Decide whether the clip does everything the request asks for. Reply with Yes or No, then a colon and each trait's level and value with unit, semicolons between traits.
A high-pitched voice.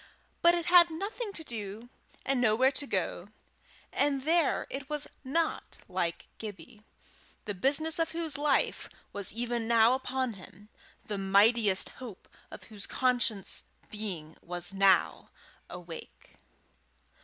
Yes: high, 235 Hz